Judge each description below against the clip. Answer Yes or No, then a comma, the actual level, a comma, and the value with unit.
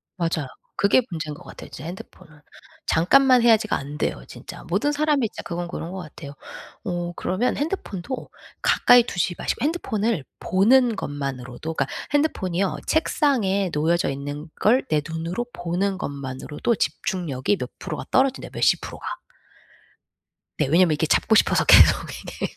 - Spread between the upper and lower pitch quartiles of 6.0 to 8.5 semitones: Yes, wide, 7.2 semitones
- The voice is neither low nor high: Yes, medium, 180 Hz